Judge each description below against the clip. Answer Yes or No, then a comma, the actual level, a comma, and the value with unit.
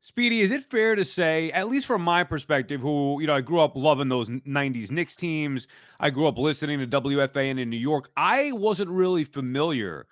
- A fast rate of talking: Yes, fast, 210 wpm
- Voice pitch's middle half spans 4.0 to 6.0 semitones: Yes, average, 4.4 semitones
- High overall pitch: No, medium, 155 Hz